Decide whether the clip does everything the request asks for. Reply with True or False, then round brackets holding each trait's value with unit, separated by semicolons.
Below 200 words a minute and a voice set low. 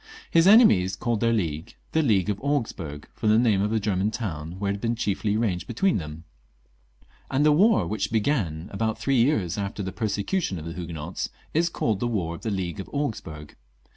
False (205 wpm; 105 Hz)